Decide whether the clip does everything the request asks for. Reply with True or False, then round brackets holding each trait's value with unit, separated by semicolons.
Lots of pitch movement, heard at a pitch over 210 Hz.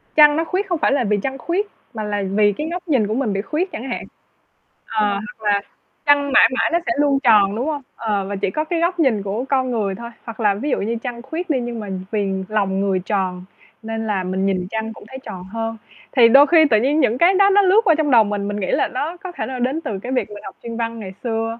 True (5.9 semitones; 230 Hz)